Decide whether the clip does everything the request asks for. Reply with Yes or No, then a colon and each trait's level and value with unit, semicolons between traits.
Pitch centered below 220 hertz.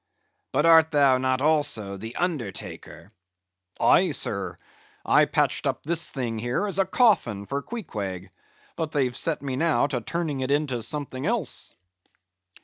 Yes: medium, 140 Hz